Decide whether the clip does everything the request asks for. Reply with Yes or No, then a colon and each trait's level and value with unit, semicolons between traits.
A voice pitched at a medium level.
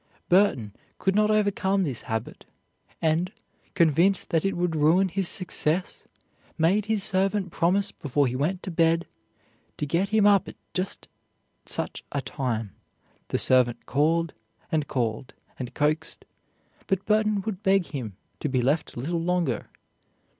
Yes: medium, 170 Hz